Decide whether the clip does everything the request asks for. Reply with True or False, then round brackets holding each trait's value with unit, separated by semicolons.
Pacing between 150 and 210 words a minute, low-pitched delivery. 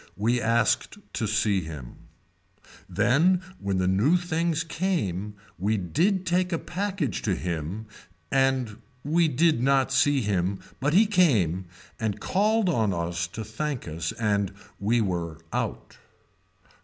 False (135 wpm; 115 Hz)